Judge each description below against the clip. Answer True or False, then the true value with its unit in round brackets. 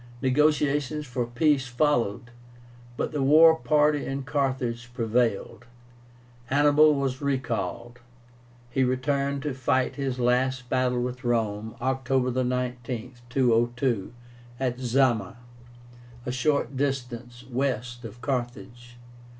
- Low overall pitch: True (125 Hz)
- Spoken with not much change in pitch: True (2.3 semitones)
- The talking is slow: True (105 wpm)